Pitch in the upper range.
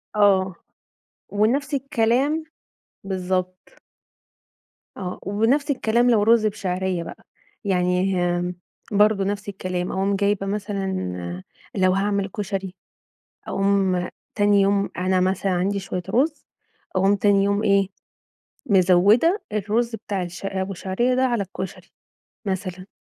Yes: high, 200 Hz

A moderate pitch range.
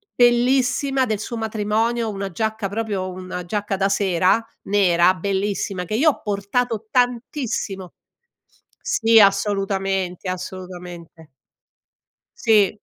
Yes: average, 3.3 semitones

